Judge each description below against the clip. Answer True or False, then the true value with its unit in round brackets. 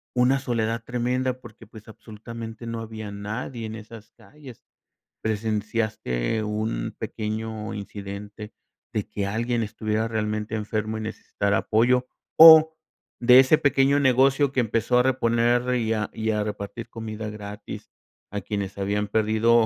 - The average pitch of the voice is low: True (110 Hz)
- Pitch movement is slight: True (2.2 semitones)